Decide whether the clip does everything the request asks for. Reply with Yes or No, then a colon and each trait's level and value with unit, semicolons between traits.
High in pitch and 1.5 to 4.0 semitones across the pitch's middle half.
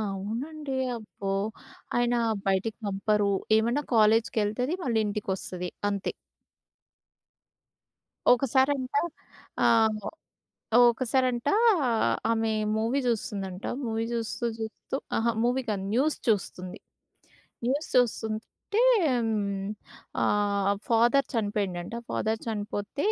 Yes: high, 225 Hz; average, 3.1 semitones